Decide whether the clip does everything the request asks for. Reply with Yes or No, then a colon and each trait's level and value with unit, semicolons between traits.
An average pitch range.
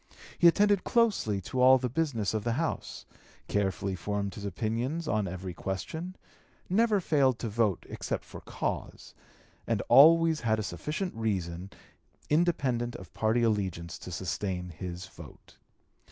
No: wide, 8.0 semitones